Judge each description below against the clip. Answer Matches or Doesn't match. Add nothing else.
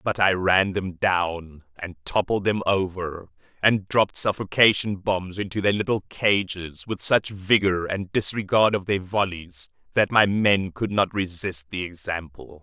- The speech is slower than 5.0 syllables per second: Matches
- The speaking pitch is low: Matches